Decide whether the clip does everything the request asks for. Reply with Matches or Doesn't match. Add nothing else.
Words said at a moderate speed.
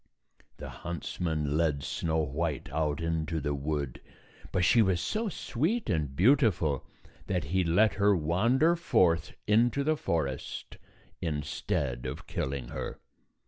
Doesn't match